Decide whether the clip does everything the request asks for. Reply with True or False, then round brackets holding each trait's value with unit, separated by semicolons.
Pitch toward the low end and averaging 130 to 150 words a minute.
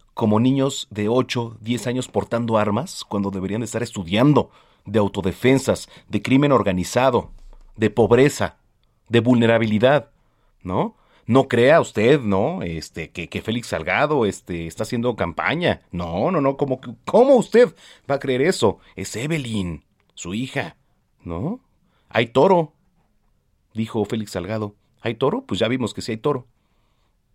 True (115 Hz; 145 wpm)